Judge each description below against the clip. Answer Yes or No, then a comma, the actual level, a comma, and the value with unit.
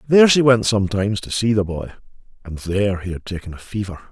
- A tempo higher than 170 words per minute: Yes, fast, 205 wpm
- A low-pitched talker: Yes, low, 105 Hz